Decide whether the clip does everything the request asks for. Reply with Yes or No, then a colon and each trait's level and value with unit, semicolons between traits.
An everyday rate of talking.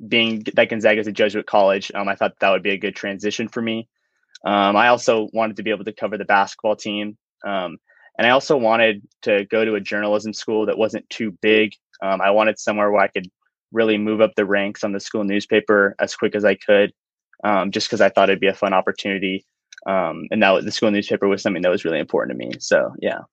No: fast, 240 wpm